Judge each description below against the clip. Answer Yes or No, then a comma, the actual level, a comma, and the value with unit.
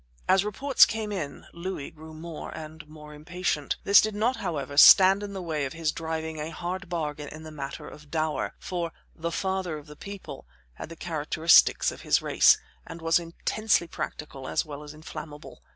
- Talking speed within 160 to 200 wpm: Yes, average, 185 wpm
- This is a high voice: No, medium, 160 Hz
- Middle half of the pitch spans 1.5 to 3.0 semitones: No, average, 3.5 semitones